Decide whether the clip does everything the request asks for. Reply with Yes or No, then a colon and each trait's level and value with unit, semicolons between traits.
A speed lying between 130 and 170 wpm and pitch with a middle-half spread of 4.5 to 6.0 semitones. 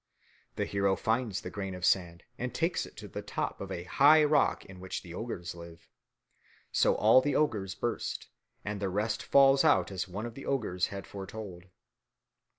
No: average, 185 wpm; average, 4.8 semitones